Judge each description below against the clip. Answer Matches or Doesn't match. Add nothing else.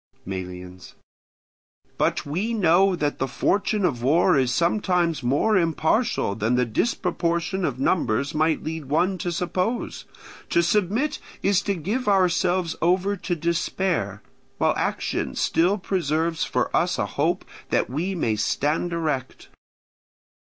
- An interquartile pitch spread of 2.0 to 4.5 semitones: Doesn't match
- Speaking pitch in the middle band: Matches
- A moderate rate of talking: Doesn't match